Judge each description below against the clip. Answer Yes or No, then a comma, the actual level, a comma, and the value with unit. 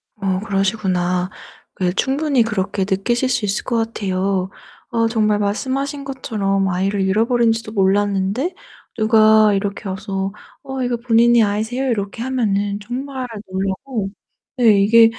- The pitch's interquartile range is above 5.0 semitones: No, average, 3.5 semitones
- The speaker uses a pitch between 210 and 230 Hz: Yes, high, 215 Hz